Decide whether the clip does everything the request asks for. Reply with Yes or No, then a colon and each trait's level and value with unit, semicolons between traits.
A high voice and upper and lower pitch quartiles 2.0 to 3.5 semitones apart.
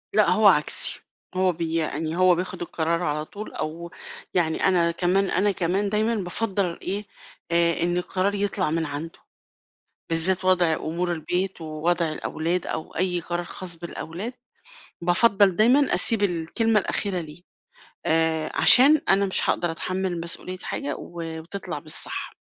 No: medium, 175 Hz; average, 2.8 semitones